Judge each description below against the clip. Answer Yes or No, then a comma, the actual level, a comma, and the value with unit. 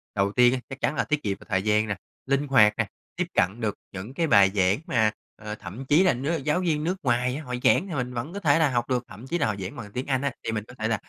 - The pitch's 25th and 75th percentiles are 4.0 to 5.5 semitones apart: Yes, average, 5.2 semitones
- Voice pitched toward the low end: Yes, low, 125 Hz